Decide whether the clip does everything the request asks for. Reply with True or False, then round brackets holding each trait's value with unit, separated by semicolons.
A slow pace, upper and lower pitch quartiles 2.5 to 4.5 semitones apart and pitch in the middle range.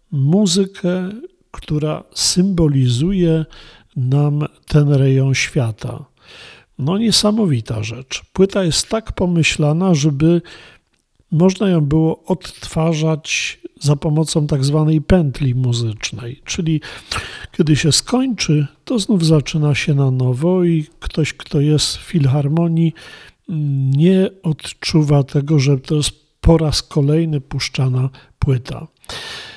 True (105 wpm; 4.1 semitones; 155 Hz)